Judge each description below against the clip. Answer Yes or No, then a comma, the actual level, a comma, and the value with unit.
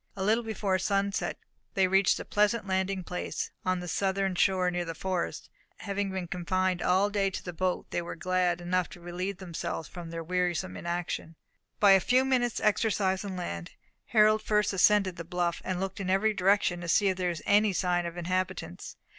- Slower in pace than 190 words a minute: No, average, 195 wpm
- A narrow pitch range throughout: Yes, narrow, 2.1 semitones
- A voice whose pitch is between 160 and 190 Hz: Yes, medium, 185 Hz